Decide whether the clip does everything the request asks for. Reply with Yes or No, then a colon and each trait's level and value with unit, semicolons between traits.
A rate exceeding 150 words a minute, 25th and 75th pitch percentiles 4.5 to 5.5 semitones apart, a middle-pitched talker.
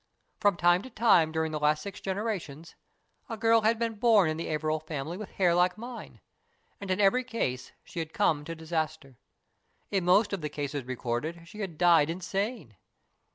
Yes: average, 185 wpm; average, 4.8 semitones; medium, 175 Hz